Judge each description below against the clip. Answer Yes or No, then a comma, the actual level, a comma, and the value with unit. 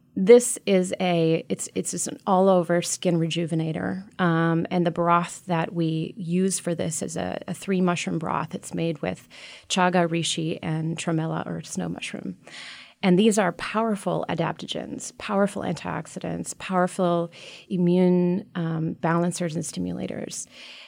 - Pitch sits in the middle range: Yes, medium, 175 Hz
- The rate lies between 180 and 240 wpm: No, average, 140 wpm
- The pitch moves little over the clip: Yes, narrow, 1.9 semitones